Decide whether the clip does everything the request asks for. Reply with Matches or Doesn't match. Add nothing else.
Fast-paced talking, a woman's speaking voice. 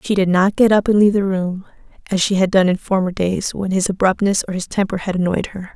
Matches